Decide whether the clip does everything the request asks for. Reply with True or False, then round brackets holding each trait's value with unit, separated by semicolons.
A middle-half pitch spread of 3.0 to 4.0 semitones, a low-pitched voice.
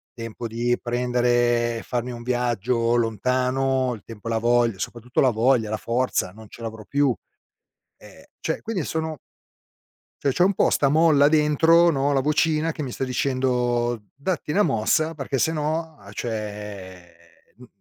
True (3.7 semitones; 125 Hz)